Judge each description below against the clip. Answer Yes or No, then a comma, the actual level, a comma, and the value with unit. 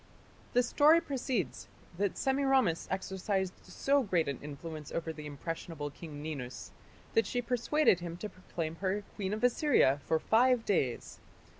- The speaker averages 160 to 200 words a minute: No, average, 145 wpm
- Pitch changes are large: Yes, wide, 7.5 semitones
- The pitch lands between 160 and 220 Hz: Yes, high, 190 Hz